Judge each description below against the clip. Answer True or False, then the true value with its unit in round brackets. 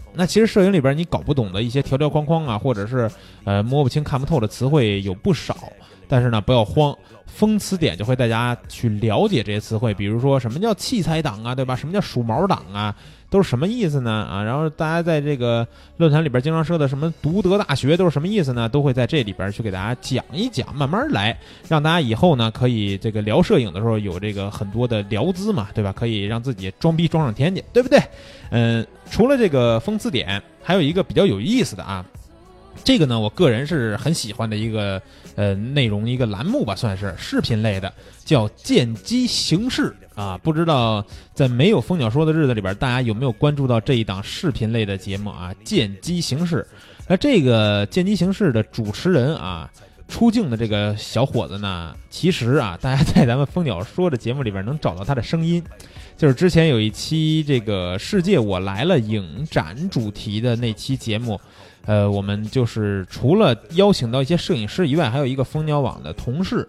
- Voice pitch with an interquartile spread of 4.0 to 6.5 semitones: False (7.0 semitones)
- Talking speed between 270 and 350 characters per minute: True (315 characters per minute)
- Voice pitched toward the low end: True (125 Hz)